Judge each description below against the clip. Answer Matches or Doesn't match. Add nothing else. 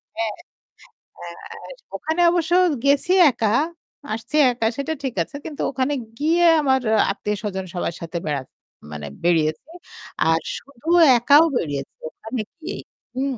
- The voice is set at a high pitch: Matches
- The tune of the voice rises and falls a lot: Matches